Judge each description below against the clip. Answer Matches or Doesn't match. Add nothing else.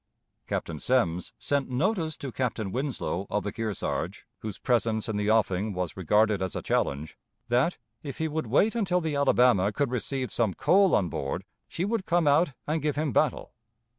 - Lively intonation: Matches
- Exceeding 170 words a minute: Matches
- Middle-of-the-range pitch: Doesn't match